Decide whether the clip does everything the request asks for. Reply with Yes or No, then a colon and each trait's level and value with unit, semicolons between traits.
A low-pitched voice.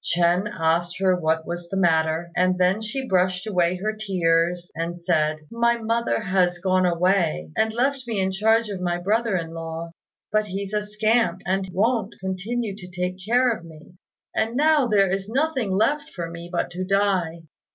No: medium, 185 Hz